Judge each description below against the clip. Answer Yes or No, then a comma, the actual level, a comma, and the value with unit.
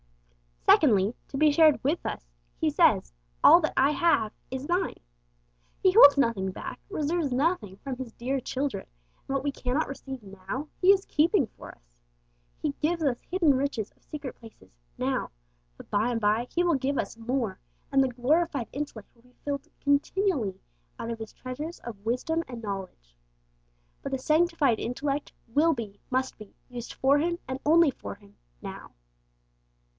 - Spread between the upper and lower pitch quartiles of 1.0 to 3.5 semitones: No, average, 5.0 semitones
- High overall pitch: Yes, very high, 265 Hz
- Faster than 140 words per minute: Yes, average, 170 wpm